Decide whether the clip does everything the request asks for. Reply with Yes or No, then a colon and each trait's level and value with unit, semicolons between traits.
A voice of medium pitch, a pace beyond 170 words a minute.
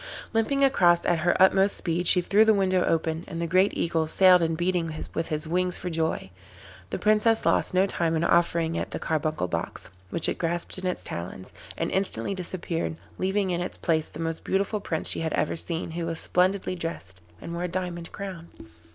Yes: medium, 175 Hz; fast, 205 wpm